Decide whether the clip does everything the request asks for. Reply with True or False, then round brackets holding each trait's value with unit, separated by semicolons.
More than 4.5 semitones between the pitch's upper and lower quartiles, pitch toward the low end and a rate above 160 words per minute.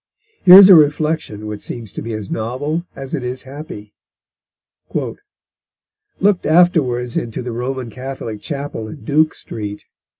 False (5.3 semitones; 130 Hz; 140 wpm)